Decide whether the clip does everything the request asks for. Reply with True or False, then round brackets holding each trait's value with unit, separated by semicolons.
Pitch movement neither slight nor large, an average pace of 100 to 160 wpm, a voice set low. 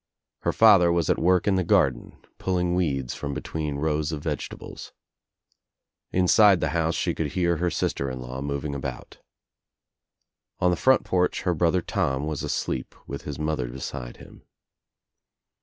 True (4.4 semitones; 155 wpm; 80 Hz)